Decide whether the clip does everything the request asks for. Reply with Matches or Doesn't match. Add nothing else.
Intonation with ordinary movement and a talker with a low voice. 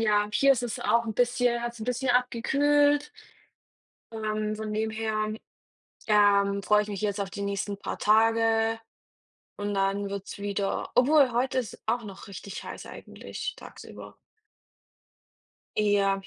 Doesn't match